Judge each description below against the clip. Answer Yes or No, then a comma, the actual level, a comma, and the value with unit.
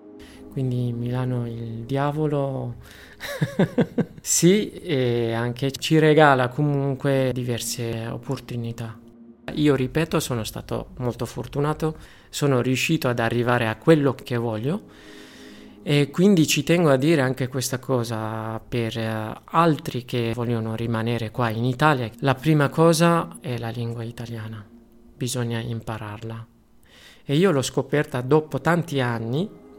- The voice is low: Yes, low, 125 Hz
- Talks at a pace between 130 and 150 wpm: No, average, 120 wpm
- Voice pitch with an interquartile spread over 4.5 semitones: No, average, 4.1 semitones